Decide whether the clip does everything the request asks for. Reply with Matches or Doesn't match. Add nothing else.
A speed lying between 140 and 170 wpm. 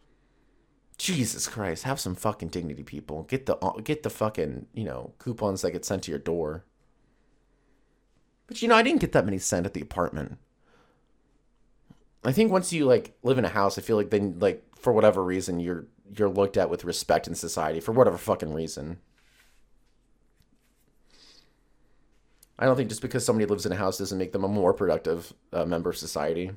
Doesn't match